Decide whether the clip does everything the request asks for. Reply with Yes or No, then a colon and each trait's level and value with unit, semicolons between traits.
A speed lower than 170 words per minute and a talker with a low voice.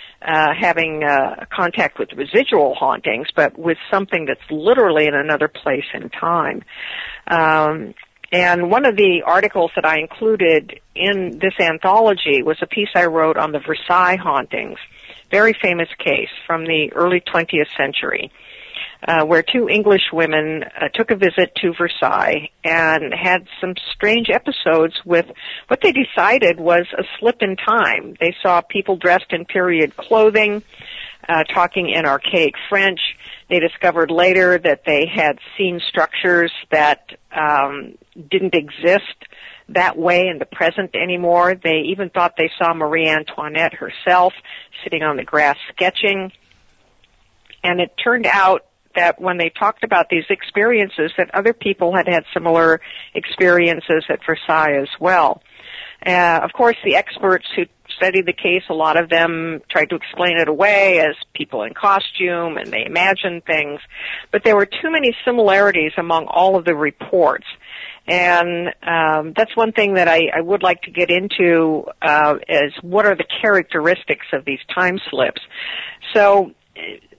No: average, 155 wpm; medium, 175 Hz